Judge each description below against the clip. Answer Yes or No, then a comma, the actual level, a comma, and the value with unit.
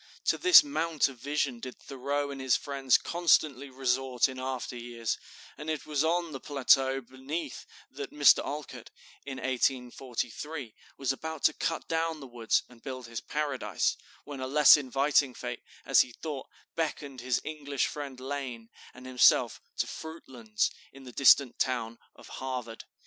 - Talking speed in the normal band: Yes, average, 160 wpm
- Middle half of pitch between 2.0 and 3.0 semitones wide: Yes, average, 2.7 semitones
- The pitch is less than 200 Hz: Yes, low, 135 Hz